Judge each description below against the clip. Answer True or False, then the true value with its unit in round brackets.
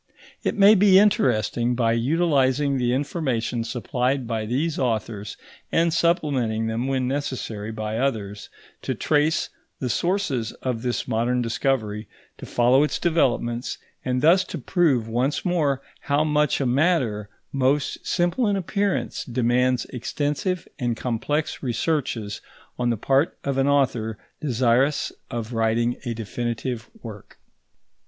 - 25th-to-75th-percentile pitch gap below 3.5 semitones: False (4.3 semitones)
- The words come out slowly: True (130 wpm)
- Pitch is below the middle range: True (130 Hz)